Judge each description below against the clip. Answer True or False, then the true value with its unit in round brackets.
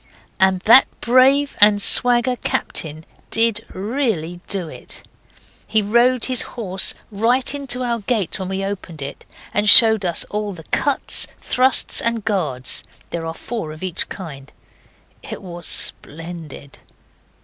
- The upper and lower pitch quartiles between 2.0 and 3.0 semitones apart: False (5.6 semitones)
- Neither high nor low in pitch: False (205 Hz)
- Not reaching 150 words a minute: True (140 wpm)